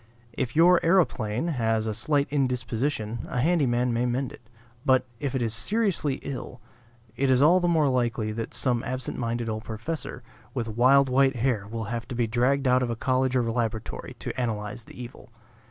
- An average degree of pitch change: Yes, average, 3.0 semitones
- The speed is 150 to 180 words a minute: No, average, 190 wpm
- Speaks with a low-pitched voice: Yes, low, 125 Hz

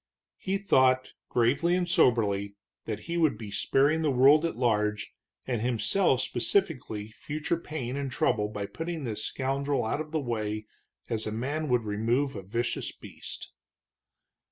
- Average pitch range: No, wide, 5.7 semitones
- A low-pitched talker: Yes, low, 125 Hz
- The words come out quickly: No, average, 155 wpm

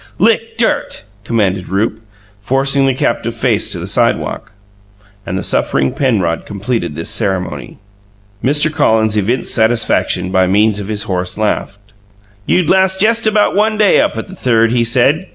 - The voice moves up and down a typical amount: No, wide, 8.1 semitones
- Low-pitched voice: Yes, low, 115 Hz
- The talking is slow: No, average, 155 wpm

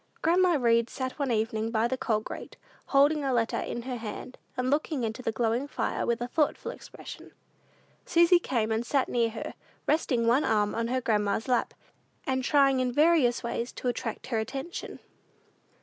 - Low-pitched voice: No, high, 245 Hz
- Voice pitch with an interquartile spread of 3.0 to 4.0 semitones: Yes, average, 3.3 semitones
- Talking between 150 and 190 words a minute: Yes, average, 180 wpm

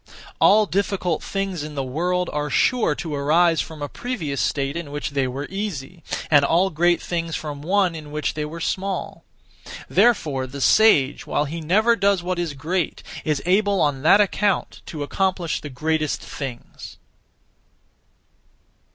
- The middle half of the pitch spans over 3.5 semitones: Yes, average, 4.4 semitones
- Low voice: No, medium, 165 Hz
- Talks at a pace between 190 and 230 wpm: No, average, 160 wpm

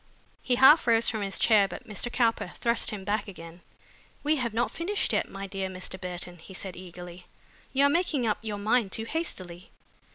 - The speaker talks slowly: No, average, 195 wpm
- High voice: Yes, high, 210 Hz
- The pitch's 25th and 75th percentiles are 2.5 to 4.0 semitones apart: No, average, 4.6 semitones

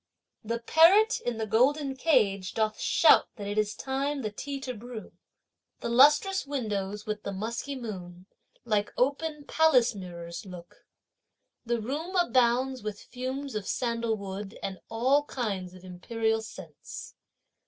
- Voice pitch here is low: No, high, 230 Hz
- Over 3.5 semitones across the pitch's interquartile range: Yes, average, 4.9 semitones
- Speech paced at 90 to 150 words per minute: Yes, average, 140 wpm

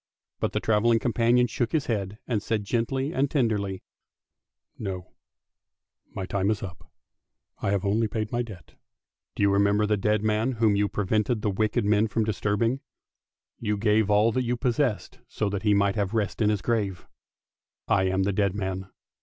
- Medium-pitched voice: No, low, 105 Hz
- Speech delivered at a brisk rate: No, average, 180 wpm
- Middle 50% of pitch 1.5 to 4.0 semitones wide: Yes, narrow, 2.4 semitones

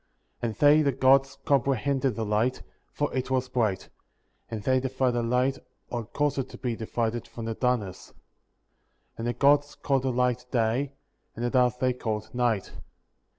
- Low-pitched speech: Yes, low, 125 Hz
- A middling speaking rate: Yes, average, 180 wpm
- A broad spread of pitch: No, narrow, 2.6 semitones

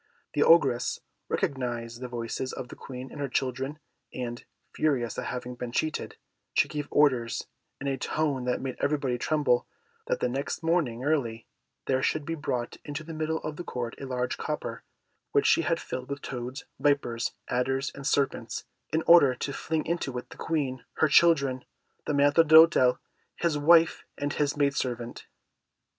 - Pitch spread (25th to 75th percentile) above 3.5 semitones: No, average, 3.2 semitones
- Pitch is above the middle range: No, low, 135 Hz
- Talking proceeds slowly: No, average, 170 wpm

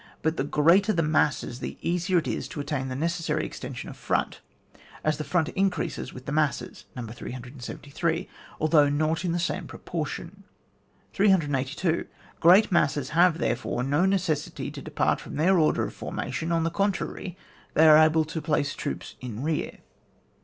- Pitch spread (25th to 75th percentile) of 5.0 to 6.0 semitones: No, average, 3.1 semitones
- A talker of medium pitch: Yes, medium, 155 Hz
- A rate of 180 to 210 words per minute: No, average, 165 wpm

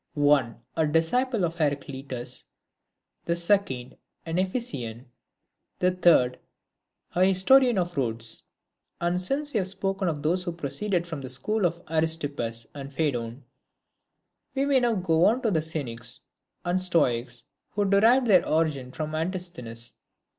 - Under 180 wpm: Yes, average, 140 wpm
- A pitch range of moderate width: No, wide, 5.7 semitones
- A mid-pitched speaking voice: Yes, medium, 165 Hz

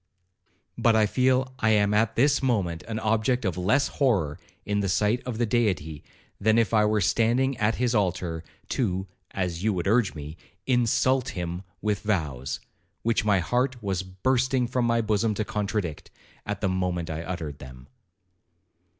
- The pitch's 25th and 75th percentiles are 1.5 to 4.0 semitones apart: No, average, 4.4 semitones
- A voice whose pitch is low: Yes, low, 105 Hz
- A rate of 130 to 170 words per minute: Yes, average, 165 wpm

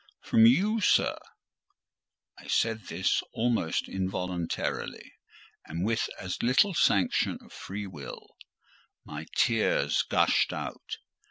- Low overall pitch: Yes, low, 100 Hz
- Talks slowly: Yes, slow, 105 wpm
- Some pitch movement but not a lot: Yes, average, 4.5 semitones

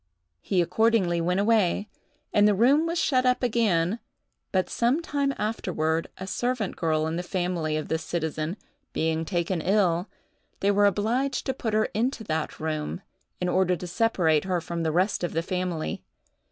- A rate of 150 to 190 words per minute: Yes, average, 170 wpm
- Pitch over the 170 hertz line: Yes, medium, 185 Hz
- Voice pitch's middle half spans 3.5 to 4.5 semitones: No, average, 5.0 semitones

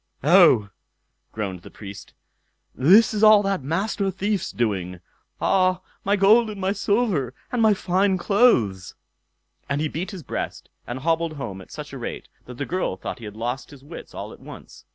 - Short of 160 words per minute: No, average, 180 wpm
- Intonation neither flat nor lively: No, wide, 8.4 semitones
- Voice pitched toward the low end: No, medium, 170 Hz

